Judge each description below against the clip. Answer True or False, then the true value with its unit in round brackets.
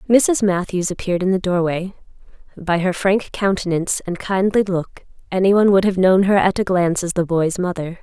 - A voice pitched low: False (185 Hz)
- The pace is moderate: True (185 wpm)